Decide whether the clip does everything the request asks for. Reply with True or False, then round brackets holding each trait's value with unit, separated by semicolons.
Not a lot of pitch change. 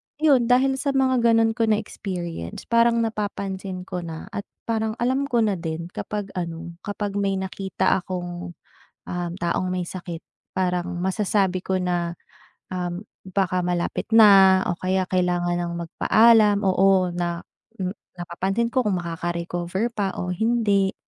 False (3.7 semitones)